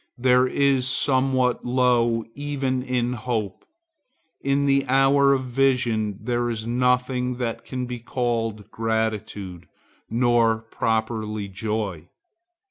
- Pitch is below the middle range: Yes, low, 120 Hz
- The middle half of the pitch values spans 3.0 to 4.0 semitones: No, narrow, 2.6 semitones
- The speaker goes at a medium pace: No, slow, 110 wpm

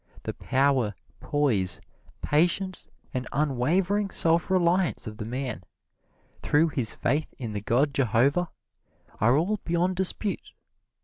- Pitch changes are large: Yes, wide, 6.3 semitones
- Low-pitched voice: No, medium, 145 Hz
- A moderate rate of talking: No, slow, 120 wpm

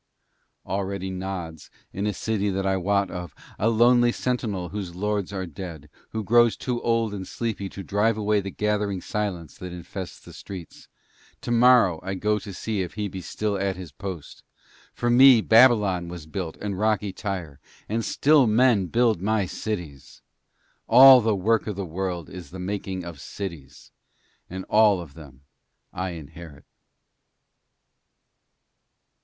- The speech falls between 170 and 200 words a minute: No, average, 155 wpm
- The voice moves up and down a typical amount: Yes, average, 3.4 semitones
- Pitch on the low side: Yes, low, 100 Hz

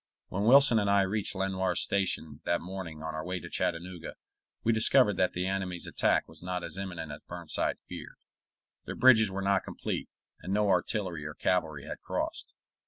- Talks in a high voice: No, very low, 95 Hz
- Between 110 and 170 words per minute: No, average, 180 wpm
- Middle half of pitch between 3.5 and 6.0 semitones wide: No, narrow, 2.6 semitones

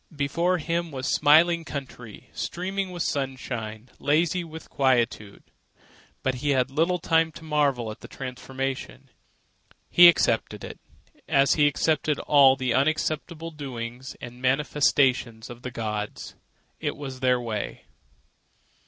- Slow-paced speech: Yes, slow, 125 wpm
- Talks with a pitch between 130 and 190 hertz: Yes, medium, 140 Hz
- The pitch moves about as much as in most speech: Yes, average, 4.0 semitones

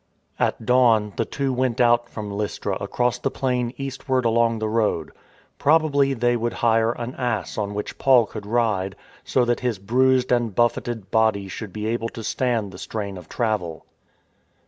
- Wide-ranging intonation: No, average, 2.8 semitones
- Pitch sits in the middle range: No, low, 115 Hz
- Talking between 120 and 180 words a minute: Yes, average, 170 wpm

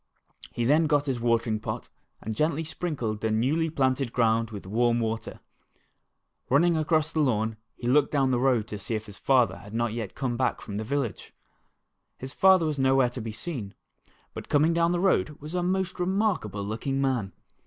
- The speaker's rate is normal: Yes, average, 185 wpm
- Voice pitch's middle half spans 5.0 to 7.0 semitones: Yes, wide, 5.5 semitones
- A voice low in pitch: Yes, low, 130 Hz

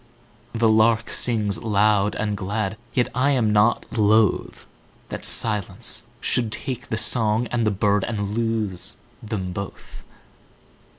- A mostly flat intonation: Yes, narrow, 2.0 semitones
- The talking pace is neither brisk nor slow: No, slow, 115 wpm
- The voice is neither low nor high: No, low, 110 Hz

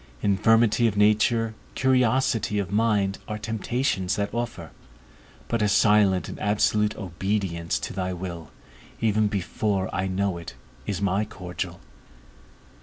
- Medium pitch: No, low, 105 Hz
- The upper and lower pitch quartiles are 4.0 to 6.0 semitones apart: No, average, 2.7 semitones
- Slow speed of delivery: Yes, slow, 125 wpm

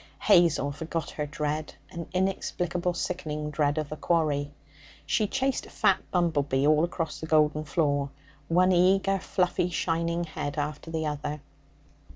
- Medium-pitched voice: Yes, medium, 160 Hz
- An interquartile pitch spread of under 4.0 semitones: Yes, average, 2.9 semitones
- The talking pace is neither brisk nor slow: Yes, average, 150 wpm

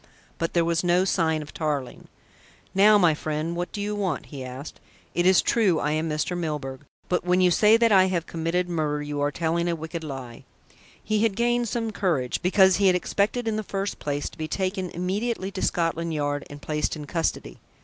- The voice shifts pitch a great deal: No, average, 4.1 semitones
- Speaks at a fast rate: Yes, fast, 210 wpm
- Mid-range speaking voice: Yes, medium, 170 Hz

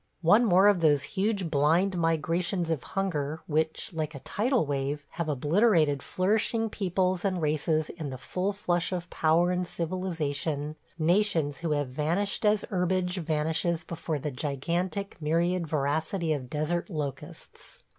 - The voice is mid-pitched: Yes, medium, 165 Hz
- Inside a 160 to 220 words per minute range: No, average, 145 wpm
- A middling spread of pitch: Yes, average, 3.5 semitones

